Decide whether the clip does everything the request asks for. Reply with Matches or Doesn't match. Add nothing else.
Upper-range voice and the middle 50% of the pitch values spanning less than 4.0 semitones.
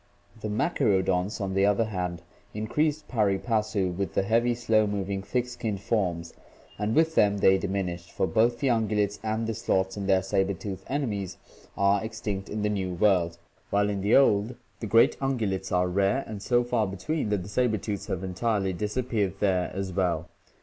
Doesn't match